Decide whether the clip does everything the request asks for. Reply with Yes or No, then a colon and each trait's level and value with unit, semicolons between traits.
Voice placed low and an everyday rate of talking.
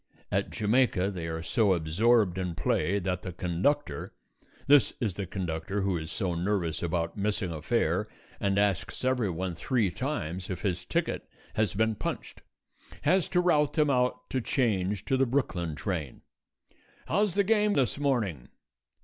Yes: low, 100 Hz; average, 160 wpm